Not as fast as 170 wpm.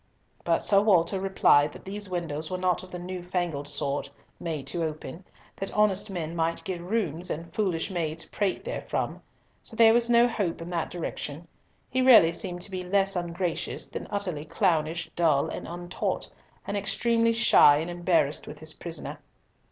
No: average, 175 wpm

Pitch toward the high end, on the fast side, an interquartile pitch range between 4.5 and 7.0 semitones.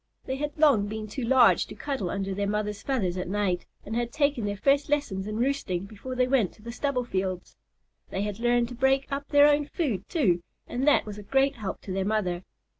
Yes: high, 230 Hz; fast, 225 wpm; wide, 5.4 semitones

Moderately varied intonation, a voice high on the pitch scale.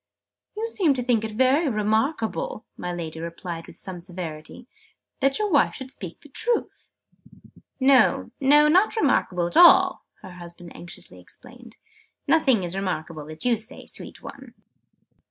No: wide, 8.5 semitones; high, 225 Hz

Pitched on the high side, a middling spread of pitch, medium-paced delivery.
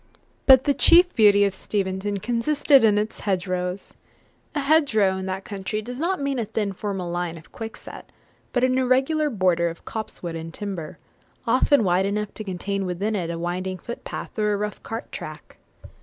Yes: high, 205 Hz; average, 4.6 semitones; average, 180 wpm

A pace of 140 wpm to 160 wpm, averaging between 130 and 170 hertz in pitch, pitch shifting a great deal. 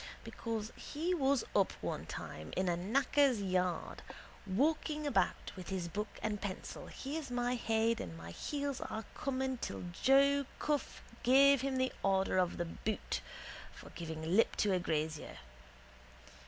No: average, 150 wpm; high, 225 Hz; wide, 6.9 semitones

